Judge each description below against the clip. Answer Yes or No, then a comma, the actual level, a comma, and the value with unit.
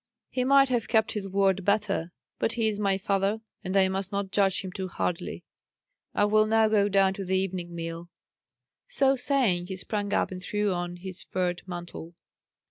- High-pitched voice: Yes, high, 195 Hz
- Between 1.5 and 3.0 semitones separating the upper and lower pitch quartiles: Yes, narrow, 2.6 semitones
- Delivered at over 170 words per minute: Yes, average, 190 wpm